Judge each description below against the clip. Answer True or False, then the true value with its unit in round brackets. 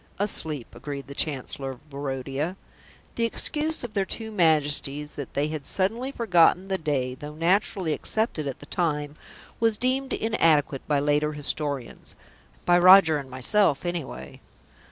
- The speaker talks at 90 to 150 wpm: True (145 wpm)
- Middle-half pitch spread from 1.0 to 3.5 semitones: False (5.5 semitones)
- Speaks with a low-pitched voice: False (155 Hz)